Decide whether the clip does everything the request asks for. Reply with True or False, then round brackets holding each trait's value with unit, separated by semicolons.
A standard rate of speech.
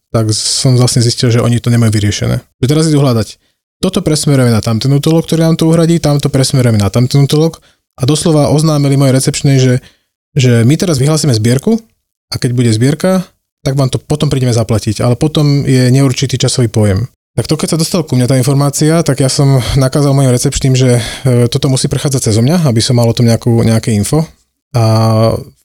False (195 wpm)